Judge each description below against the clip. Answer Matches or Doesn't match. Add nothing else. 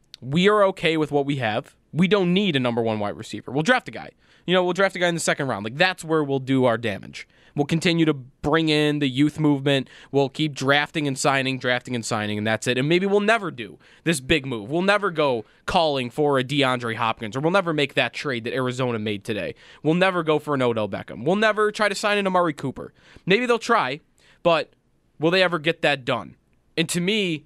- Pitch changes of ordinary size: Doesn't match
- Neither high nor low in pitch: Matches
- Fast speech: Matches